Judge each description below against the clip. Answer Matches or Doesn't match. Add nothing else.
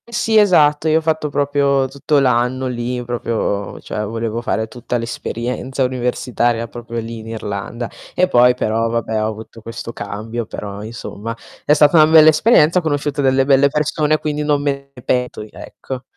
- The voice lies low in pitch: Matches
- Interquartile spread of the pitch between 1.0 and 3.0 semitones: Doesn't match